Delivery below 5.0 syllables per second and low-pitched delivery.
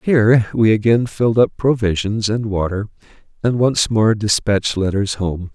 Yes: 4.8 syllables/s; low, 110 Hz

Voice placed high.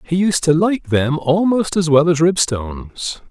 No: medium, 165 Hz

